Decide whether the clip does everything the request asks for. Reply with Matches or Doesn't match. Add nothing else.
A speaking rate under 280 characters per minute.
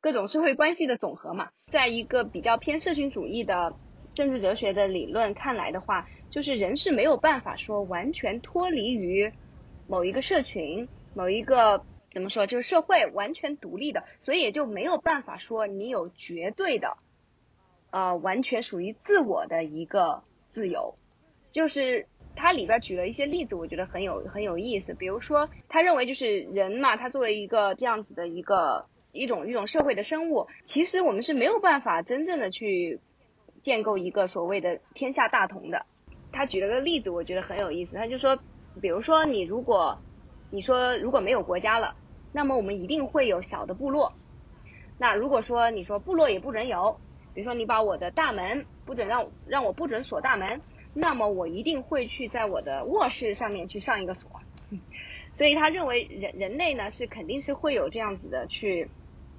Doesn't match